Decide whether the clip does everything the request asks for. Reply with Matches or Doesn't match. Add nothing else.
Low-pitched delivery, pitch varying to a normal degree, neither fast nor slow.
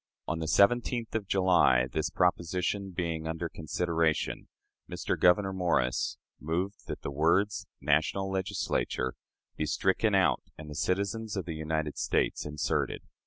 Doesn't match